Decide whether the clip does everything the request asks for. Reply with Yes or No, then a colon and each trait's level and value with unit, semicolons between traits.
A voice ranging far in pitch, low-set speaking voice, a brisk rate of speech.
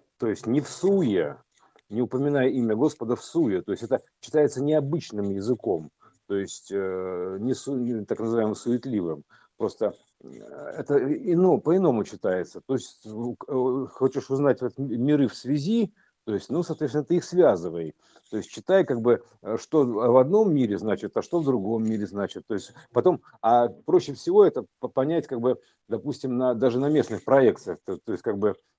Yes: wide, 6.1 semitones; low, 130 Hz; fast, 165 wpm